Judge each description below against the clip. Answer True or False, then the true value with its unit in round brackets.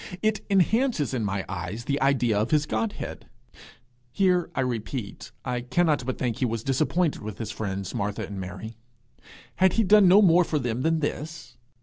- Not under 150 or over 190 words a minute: True (185 wpm)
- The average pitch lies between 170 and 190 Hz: False (130 Hz)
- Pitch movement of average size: False (7.5 semitones)